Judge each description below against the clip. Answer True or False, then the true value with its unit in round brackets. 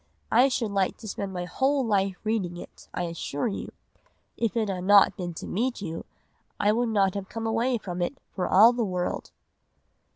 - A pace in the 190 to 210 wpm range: True (200 wpm)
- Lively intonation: False (4.0 semitones)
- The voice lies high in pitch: True (205 Hz)